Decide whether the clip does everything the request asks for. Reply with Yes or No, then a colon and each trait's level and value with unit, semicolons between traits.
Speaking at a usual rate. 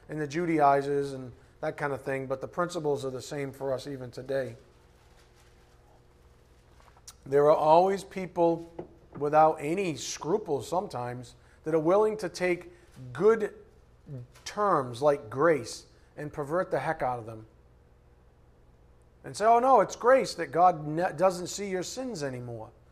Yes: average, 145 wpm